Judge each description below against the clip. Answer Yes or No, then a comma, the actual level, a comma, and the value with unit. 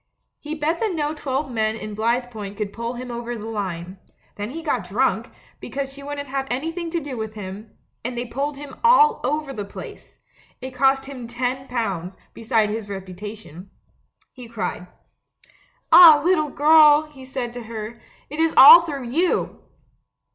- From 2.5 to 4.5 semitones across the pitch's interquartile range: No, average, 5.2 semitones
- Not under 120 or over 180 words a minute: Yes, average, 170 wpm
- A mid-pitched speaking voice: No, very high, 250 Hz